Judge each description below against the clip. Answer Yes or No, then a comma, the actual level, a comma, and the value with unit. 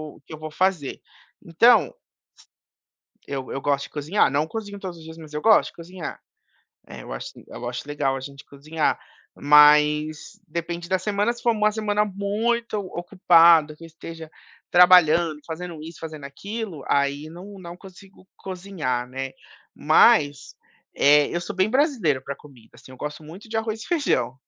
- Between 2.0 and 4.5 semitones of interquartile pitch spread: No, average, 5.2 semitones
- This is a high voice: No, medium, 165 Hz